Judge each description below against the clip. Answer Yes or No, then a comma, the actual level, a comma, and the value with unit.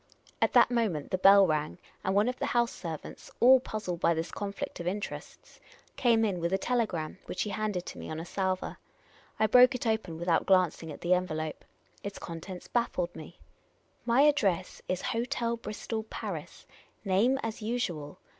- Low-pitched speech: No, high, 195 Hz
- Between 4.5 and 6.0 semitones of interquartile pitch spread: Yes, average, 5.0 semitones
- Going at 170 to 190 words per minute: Yes, average, 185 wpm